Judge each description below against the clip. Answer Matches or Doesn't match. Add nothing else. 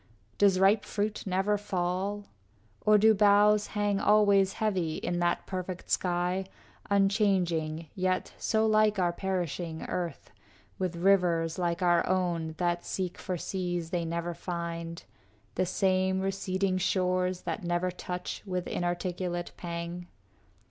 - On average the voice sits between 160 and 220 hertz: Matches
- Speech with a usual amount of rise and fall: Doesn't match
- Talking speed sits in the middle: Doesn't match